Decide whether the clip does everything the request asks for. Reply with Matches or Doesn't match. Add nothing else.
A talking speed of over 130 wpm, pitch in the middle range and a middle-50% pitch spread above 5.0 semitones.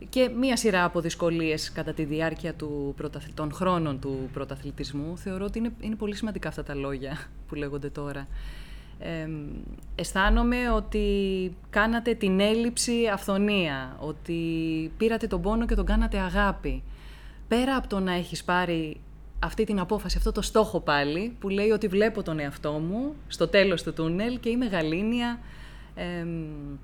Matches